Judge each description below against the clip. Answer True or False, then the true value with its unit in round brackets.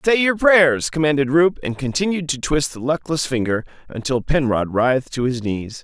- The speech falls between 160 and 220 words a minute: True (185 wpm)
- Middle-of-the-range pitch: True (145 Hz)